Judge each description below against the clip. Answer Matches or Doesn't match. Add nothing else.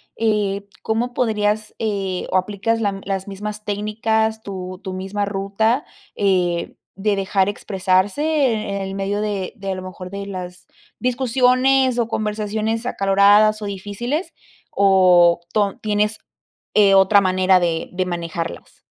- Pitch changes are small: Matches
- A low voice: Doesn't match